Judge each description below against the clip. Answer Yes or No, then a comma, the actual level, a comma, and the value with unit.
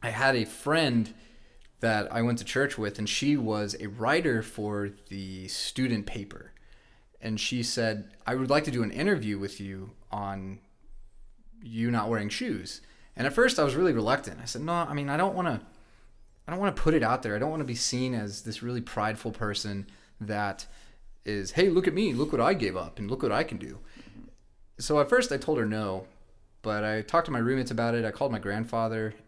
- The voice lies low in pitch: Yes, low, 110 Hz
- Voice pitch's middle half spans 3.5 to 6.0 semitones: Yes, average, 3.9 semitones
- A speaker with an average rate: No, fast, 220 wpm